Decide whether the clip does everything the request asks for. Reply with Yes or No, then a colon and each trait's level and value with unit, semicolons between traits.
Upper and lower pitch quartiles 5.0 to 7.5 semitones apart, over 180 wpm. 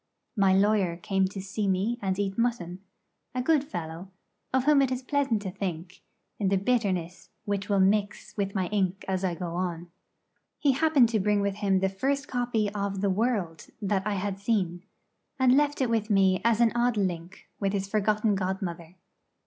No: average, 3.5 semitones; average, 190 wpm